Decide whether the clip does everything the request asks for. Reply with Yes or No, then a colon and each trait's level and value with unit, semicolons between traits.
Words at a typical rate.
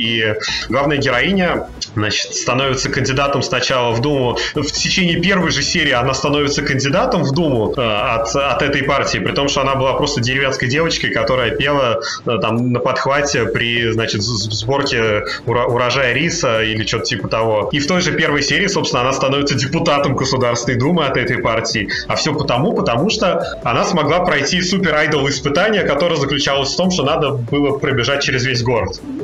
No: fast, 170 wpm